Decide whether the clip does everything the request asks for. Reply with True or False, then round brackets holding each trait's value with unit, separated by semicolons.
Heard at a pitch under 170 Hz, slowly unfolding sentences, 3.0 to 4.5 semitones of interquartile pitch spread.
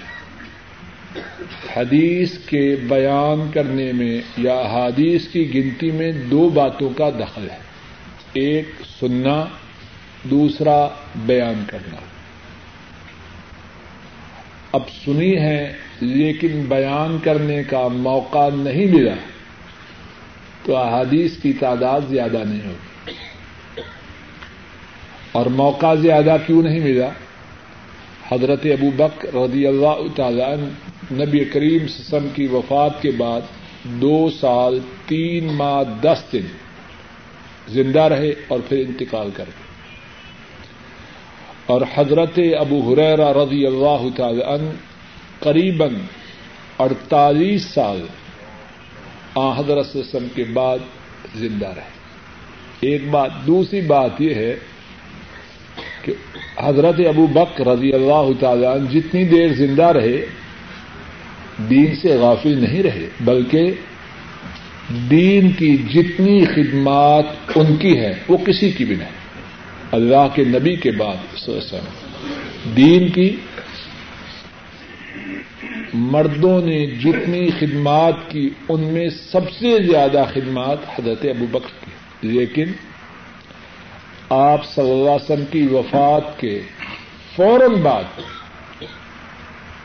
True (140 Hz; 105 wpm; 3.9 semitones)